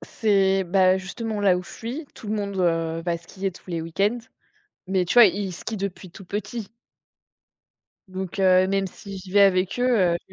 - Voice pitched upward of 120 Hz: Yes, high, 190 Hz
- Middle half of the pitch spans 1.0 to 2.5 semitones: Yes, narrow, 2.0 semitones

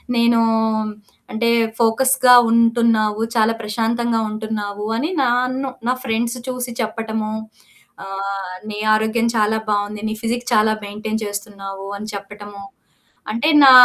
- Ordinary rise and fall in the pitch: No, narrow, 2.1 semitones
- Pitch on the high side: Yes, high, 220 Hz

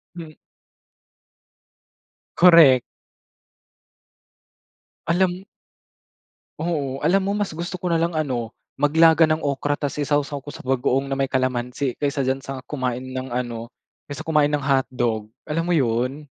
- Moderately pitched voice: Yes, medium, 145 Hz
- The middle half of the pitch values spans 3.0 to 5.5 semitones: Yes, average, 3.8 semitones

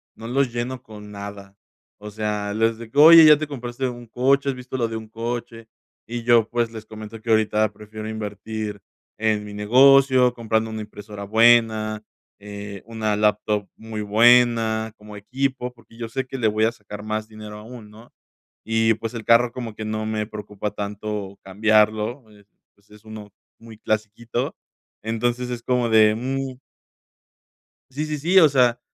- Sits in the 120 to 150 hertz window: No, low, 110 Hz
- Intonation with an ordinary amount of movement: No, narrow, 2.2 semitones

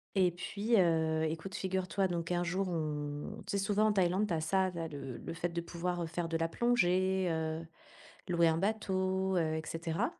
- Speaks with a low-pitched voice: No, medium, 175 Hz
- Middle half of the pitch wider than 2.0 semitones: Yes, average, 2.7 semitones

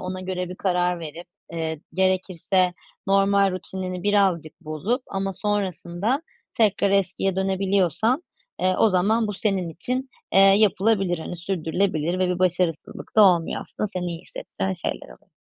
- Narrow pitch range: Yes, narrow, 2.0 semitones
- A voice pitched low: No, medium, 185 Hz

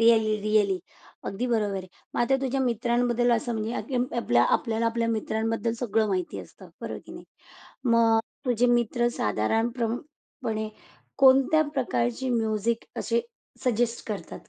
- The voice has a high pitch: Yes, high, 230 Hz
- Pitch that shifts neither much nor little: No, narrow, 1.9 semitones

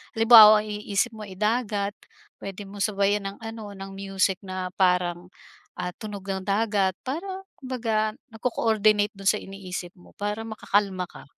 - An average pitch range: No, narrow, 2.0 semitones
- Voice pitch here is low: No, high, 205 Hz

